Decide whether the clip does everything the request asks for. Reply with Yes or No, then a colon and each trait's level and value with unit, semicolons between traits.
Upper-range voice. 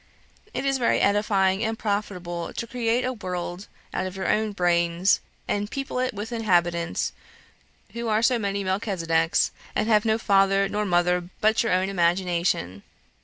Yes: high, 195 Hz